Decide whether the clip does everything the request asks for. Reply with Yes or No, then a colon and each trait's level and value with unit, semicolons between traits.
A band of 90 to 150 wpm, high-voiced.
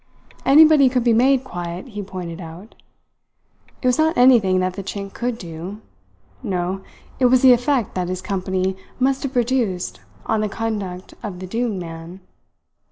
No: average, 165 wpm; high, 205 Hz